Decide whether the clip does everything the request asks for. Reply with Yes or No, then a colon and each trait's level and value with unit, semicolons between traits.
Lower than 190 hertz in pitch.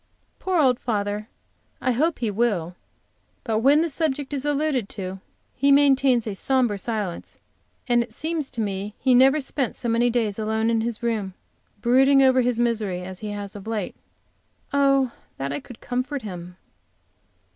No: high, 235 Hz